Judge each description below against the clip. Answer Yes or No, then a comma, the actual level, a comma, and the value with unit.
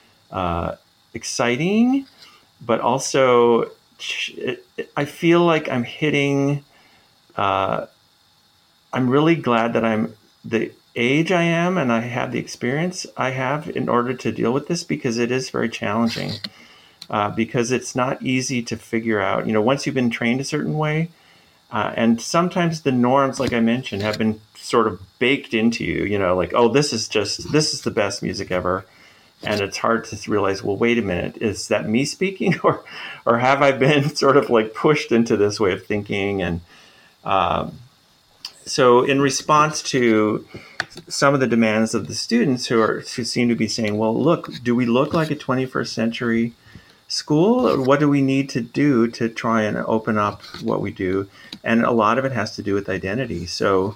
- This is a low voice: Yes, low, 120 Hz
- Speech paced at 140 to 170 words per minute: No, average, 185 wpm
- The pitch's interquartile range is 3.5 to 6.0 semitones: Yes, average, 4.3 semitones